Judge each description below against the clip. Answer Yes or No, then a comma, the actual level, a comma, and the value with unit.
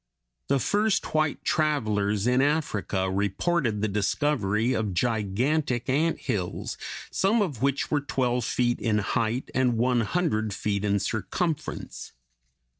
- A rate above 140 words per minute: No, slow, 135 wpm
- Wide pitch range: Yes, wide, 5.8 semitones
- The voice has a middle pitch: No, low, 120 Hz